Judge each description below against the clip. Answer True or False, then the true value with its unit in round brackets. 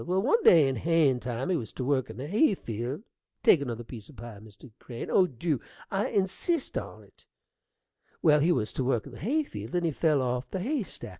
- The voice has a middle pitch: True (145 Hz)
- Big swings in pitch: True (6.9 semitones)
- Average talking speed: False (225 wpm)